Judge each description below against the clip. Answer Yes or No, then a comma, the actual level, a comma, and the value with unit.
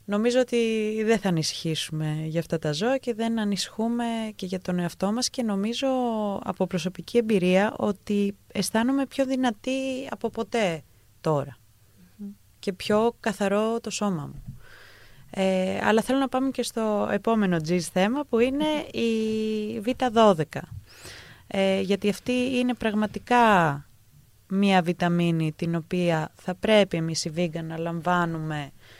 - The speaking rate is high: No, average, 135 wpm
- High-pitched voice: Yes, high, 200 Hz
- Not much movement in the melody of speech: No, average, 5.3 semitones